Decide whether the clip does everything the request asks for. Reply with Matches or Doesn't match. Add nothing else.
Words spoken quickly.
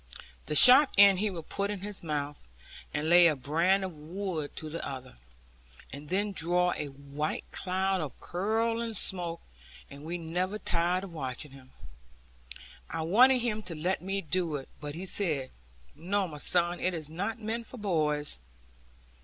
Doesn't match